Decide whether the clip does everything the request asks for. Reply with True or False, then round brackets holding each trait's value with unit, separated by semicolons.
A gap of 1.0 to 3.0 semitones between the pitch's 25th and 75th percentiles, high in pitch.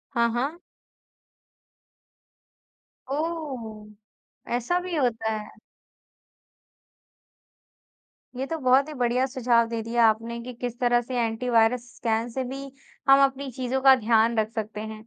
True (2.7 semitones; 240 Hz)